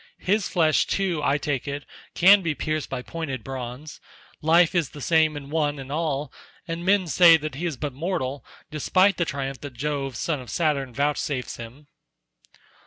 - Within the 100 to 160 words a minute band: No, average, 175 wpm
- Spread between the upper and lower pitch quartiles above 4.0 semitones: No, average, 3.5 semitones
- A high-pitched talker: No, medium, 150 Hz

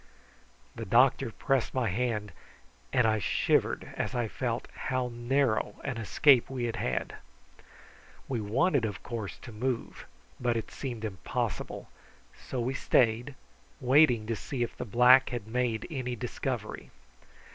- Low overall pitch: Yes, low, 120 Hz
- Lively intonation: No, average, 2.7 semitones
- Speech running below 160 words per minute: Yes, average, 145 wpm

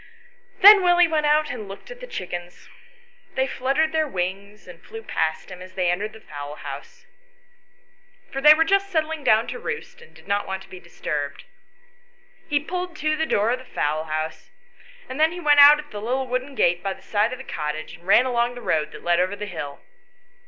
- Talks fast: Yes, fast, 215 wpm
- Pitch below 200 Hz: No, high, 245 Hz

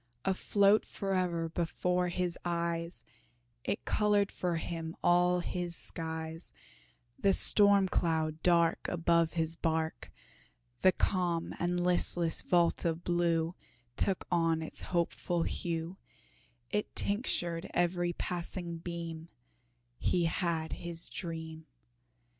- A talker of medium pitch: Yes, medium, 170 Hz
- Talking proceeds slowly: Yes, slow, 105 wpm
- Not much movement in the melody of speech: Yes, narrow, 1.4 semitones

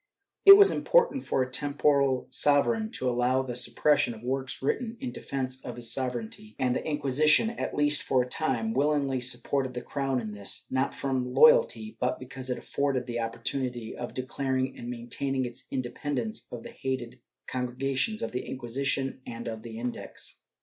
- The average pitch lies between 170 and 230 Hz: No, low, 130 Hz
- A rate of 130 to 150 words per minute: No, average, 175 wpm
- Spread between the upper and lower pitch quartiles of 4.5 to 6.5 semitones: No, narrow, 2.5 semitones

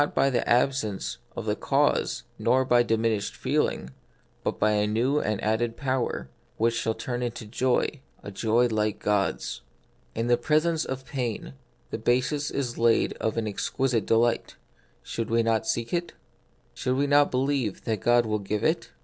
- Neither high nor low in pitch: No, low, 120 Hz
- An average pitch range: Yes, average, 3.0 semitones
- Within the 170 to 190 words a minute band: Yes, average, 175 wpm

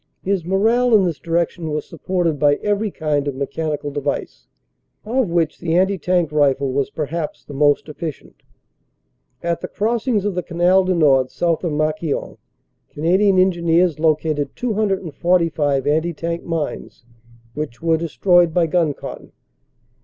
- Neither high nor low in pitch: Yes, medium, 165 Hz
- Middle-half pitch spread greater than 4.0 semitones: No, average, 3.5 semitones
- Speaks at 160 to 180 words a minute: No, average, 145 wpm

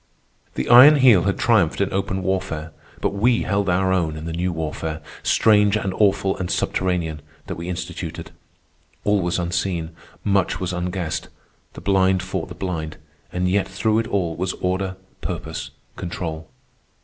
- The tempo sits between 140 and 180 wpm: Yes, average, 160 wpm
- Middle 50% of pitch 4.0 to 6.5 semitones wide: No, narrow, 2.6 semitones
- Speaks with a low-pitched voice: Yes, very low, 95 Hz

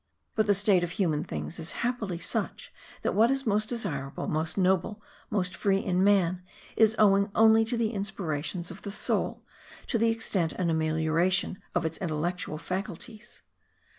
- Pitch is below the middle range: No, high, 190 Hz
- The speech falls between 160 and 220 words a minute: Yes, average, 165 wpm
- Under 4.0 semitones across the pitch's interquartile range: No, average, 4.3 semitones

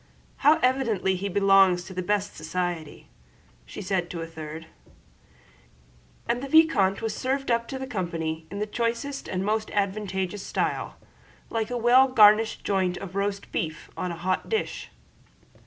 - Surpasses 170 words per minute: No, average, 155 wpm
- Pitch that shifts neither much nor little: Yes, average, 4.4 semitones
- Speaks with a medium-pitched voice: No, high, 200 Hz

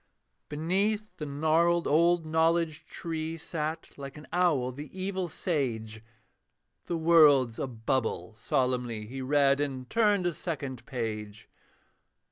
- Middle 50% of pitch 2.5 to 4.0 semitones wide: No, average, 4.7 semitones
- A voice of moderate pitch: Yes, medium, 150 Hz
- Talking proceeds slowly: Yes, slow, 120 wpm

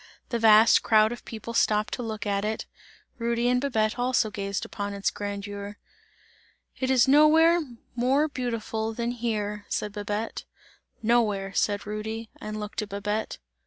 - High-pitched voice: Yes, high, 220 Hz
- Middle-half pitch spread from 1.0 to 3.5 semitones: Yes, narrow, 2.6 semitones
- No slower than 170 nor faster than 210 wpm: No, average, 150 wpm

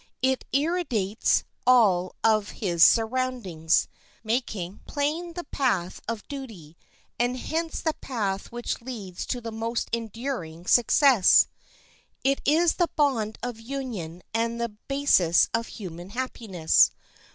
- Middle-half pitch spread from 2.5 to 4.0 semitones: No, wide, 5.5 semitones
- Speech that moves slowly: Yes, slow, 120 wpm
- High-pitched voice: Yes, high, 230 Hz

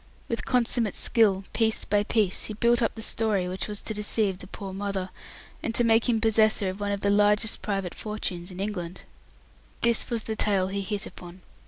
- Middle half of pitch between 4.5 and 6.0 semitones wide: No, narrow, 2.6 semitones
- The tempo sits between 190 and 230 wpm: Yes, average, 200 wpm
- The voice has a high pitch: Yes, high, 205 Hz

